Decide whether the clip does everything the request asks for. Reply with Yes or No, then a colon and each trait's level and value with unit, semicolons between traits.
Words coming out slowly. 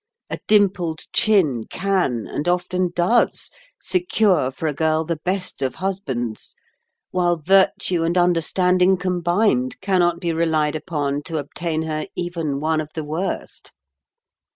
Yes: slow, 130 wpm